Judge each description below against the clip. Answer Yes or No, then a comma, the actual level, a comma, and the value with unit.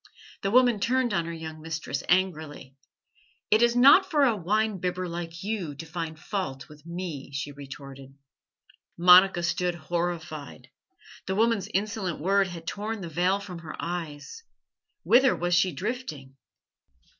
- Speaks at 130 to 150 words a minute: Yes, average, 145 wpm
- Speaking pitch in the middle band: Yes, medium, 175 Hz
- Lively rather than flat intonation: No, average, 4.3 semitones